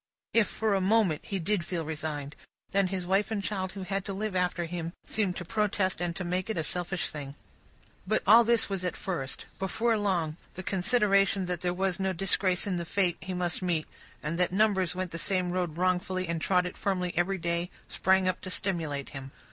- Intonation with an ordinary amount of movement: No, narrow, 2.1 semitones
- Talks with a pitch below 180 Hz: No, medium, 185 Hz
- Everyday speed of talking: No, fast, 210 wpm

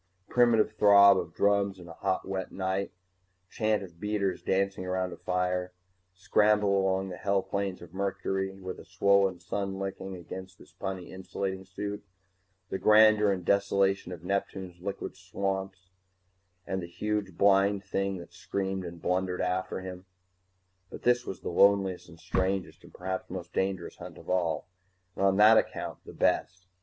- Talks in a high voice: No, very low, 95 Hz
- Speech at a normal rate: Yes, average, 165 wpm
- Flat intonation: Yes, narrow, 1.3 semitones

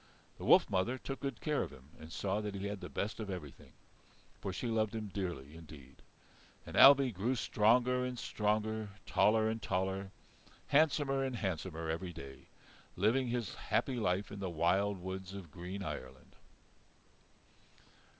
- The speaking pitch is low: Yes, low, 100 Hz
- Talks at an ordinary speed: Yes, average, 160 wpm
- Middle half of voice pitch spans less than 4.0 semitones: No, average, 4.3 semitones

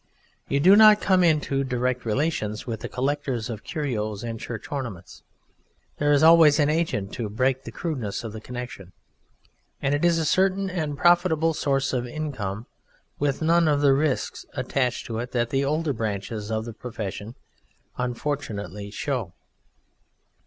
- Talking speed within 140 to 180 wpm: Yes, average, 160 wpm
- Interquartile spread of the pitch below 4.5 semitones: No, average, 5.3 semitones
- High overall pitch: No, low, 135 Hz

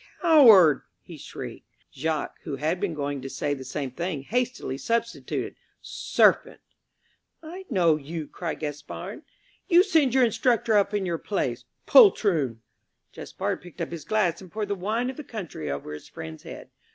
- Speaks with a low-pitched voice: No, medium, 180 Hz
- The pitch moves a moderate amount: No, wide, 7.9 semitones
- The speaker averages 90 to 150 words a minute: No, average, 165 wpm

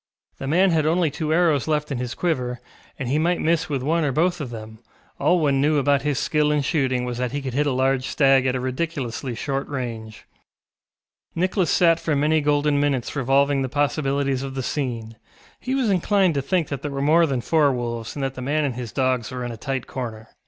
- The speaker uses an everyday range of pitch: Yes, average, 3.3 semitones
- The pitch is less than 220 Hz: Yes, medium, 140 Hz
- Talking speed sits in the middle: No, fast, 225 wpm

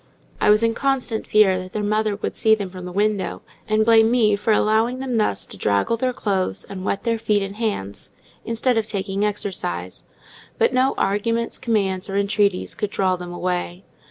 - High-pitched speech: Yes, high, 210 Hz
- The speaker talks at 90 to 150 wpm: No, average, 190 wpm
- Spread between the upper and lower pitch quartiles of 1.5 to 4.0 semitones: Yes, average, 2.9 semitones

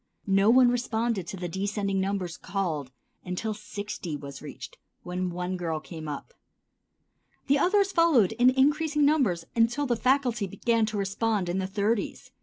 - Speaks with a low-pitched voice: No, high, 205 Hz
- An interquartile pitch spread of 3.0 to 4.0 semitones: No, average, 5.2 semitones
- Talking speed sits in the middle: Yes, average, 155 wpm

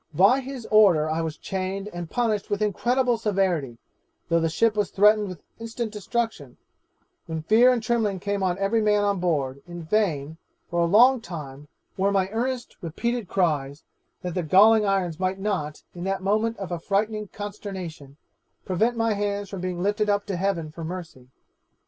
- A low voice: No, high, 195 Hz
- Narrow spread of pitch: No, average, 3.9 semitones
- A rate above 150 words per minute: Yes, average, 175 wpm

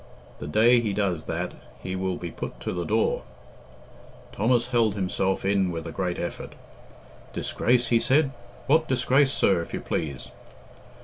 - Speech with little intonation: No, average, 5.1 semitones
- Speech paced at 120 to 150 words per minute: No, average, 160 wpm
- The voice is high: No, low, 100 Hz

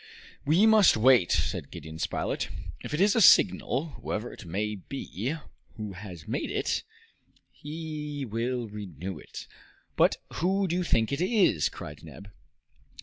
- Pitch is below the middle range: Yes, low, 125 Hz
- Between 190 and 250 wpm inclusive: No, average, 145 wpm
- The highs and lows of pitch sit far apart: Yes, wide, 8.1 semitones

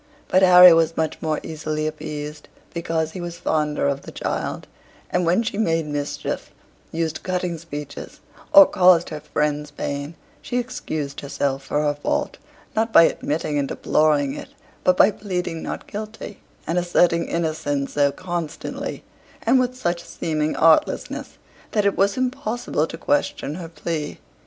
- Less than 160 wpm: Yes, average, 150 wpm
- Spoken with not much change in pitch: No, average, 3.4 semitones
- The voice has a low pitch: No, medium, 165 Hz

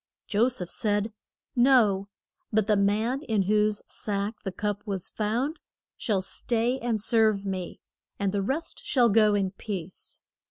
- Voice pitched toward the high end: Yes, high, 210 Hz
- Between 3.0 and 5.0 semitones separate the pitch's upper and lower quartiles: No, narrow, 2.6 semitones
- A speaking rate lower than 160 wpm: Yes, average, 150 wpm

